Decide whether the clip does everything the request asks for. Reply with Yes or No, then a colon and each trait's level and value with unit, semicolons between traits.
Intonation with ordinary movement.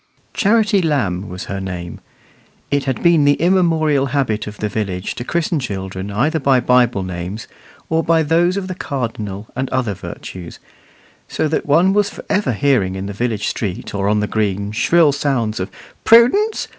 No: wide, 8.1 semitones